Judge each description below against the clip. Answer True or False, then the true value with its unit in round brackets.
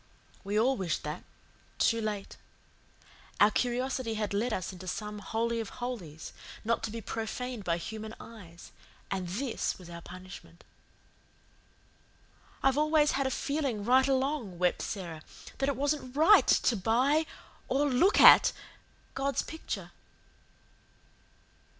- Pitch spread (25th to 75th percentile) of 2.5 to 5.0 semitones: False (5.5 semitones)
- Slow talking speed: True (130 wpm)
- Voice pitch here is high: True (230 Hz)